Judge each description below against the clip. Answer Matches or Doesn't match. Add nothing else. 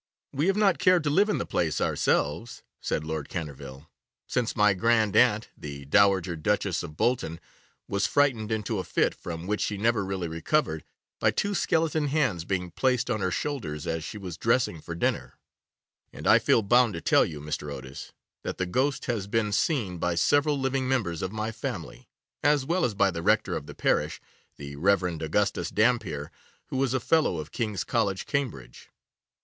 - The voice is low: Matches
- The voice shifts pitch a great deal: Matches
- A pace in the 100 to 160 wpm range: Doesn't match